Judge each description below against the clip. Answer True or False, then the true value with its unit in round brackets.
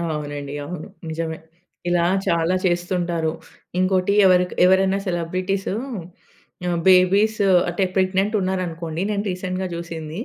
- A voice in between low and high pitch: True (180 Hz)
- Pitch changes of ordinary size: False (2.1 semitones)